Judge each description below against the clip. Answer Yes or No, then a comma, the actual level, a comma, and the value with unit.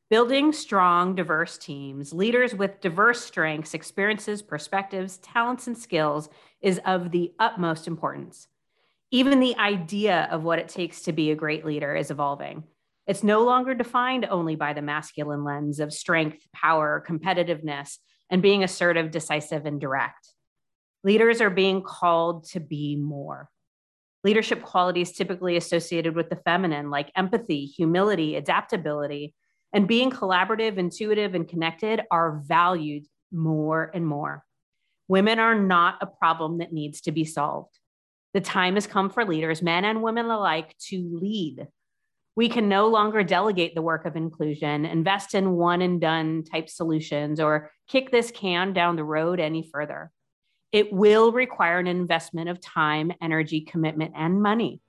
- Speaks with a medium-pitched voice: Yes, medium, 175 Hz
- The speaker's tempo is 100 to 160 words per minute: Yes, average, 150 wpm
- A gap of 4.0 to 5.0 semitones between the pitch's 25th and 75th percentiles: Yes, average, 4.3 semitones